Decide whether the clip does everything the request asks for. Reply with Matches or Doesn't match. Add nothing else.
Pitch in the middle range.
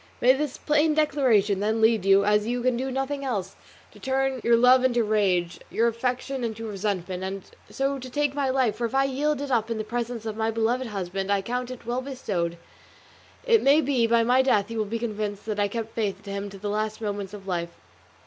Doesn't match